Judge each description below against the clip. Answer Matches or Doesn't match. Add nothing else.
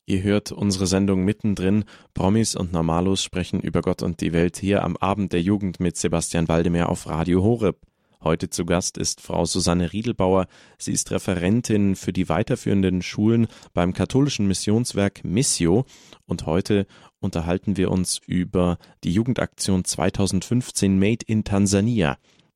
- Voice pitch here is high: Doesn't match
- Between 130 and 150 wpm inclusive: Matches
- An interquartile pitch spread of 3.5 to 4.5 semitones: Doesn't match